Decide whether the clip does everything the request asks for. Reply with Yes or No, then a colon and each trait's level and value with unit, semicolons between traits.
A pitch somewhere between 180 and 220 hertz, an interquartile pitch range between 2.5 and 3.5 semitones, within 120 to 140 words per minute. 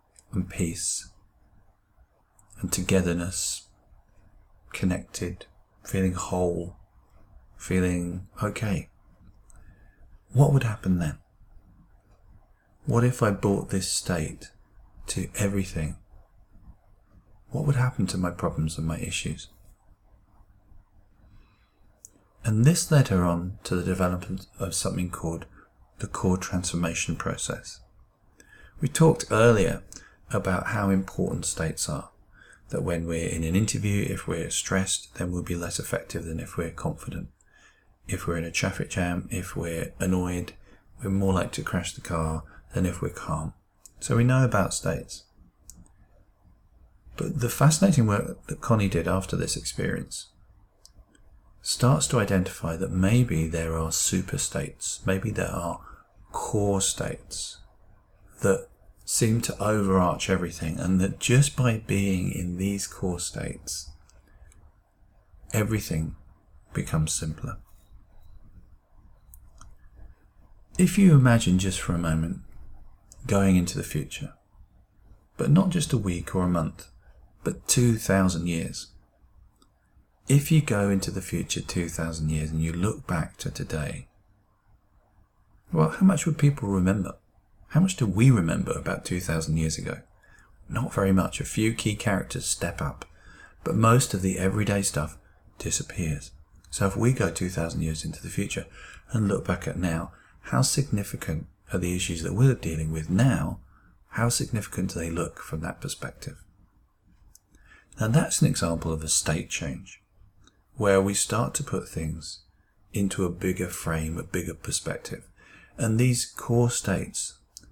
No: very low, 95 Hz; average, 3.2 semitones; slow, 135 wpm